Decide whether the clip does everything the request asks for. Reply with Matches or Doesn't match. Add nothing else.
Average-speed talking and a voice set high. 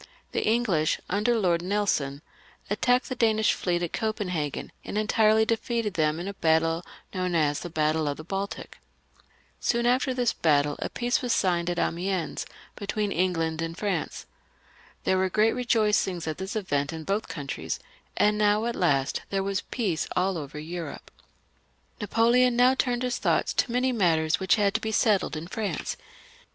Matches